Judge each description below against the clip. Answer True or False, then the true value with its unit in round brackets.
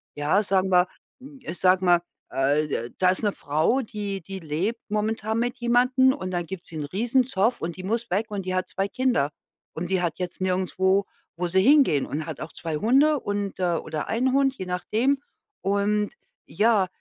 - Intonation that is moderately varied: True (4.7 semitones)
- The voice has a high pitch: True (195 Hz)